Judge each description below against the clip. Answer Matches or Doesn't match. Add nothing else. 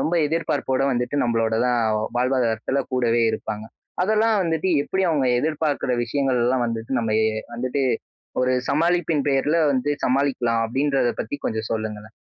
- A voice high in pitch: Doesn't match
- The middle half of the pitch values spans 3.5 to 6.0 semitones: Matches